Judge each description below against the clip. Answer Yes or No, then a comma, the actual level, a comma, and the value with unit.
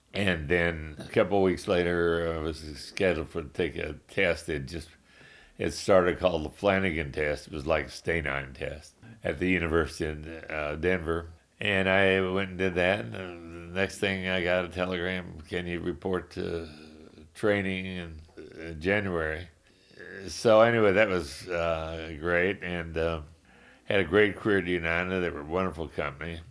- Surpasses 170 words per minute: No, average, 165 wpm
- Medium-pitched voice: No, very low, 85 Hz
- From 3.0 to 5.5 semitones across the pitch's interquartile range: No, narrow, 2.6 semitones